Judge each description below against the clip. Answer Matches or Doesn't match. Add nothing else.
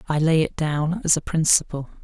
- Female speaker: Doesn't match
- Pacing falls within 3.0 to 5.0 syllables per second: Doesn't match